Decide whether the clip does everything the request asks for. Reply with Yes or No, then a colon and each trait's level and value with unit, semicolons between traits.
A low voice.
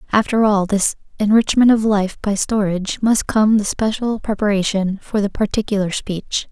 No: high, 205 Hz